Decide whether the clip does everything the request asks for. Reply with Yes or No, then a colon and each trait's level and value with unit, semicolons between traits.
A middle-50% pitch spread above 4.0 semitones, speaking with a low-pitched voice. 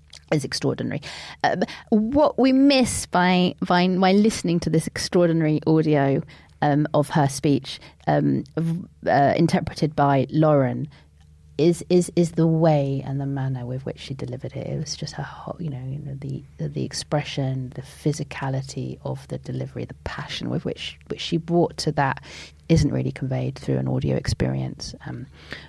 No: average, 4.6 semitones; medium, 145 Hz